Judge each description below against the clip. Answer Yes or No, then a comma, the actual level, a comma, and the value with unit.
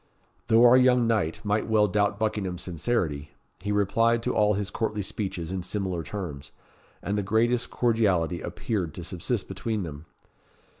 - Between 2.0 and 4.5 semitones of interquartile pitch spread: Yes, average, 3.9 semitones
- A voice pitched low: Yes, low, 105 Hz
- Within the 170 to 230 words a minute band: No, average, 155 wpm